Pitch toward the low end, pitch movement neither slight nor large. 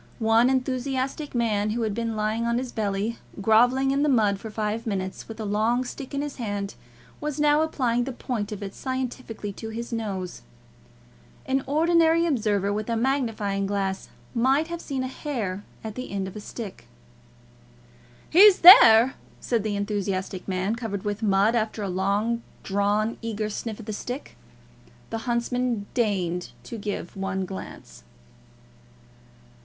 No: high, 225 Hz; average, 3.9 semitones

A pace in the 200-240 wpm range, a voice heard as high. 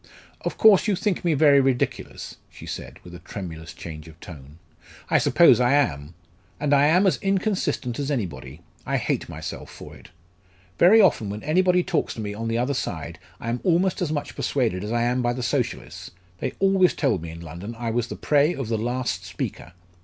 No: fast, 205 wpm; low, 125 Hz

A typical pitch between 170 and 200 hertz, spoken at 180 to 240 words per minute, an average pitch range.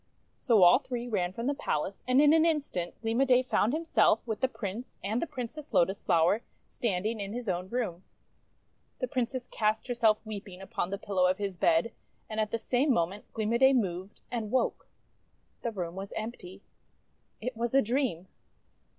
No: high, 220 Hz; average, 190 wpm; average, 4.6 semitones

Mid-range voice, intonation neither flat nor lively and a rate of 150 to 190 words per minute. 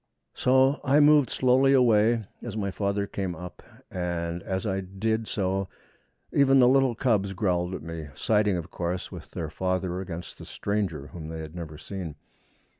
No: very low, 95 Hz; average, 4.5 semitones; average, 170 wpm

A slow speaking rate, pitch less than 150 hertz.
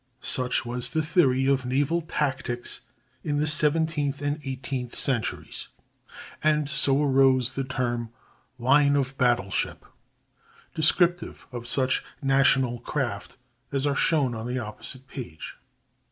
Yes: slow, 125 wpm; low, 135 Hz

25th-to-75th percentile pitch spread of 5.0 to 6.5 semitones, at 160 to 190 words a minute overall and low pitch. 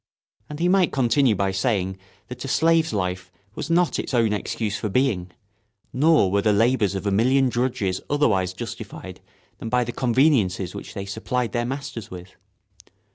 Yes: wide, 5.4 semitones; average, 170 wpm; low, 115 Hz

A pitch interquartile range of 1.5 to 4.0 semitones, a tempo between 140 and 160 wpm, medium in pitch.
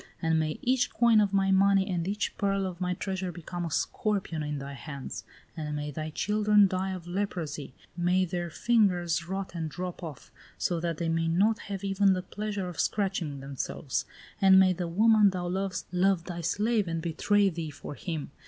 No: average, 3.2 semitones; average, 190 wpm; medium, 180 Hz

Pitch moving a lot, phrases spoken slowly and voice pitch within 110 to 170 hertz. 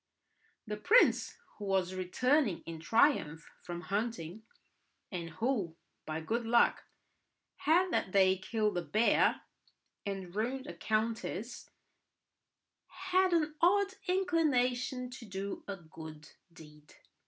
No: wide, 6.7 semitones; slow, 115 wpm; high, 215 Hz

